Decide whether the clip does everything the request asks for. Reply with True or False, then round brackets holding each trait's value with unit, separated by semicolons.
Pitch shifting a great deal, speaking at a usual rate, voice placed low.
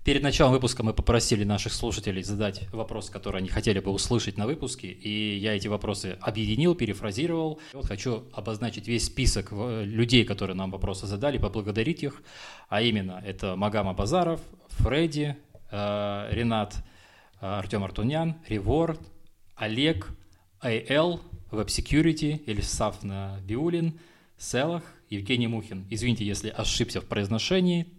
False (4.2 semitones; 125 wpm; 110 Hz)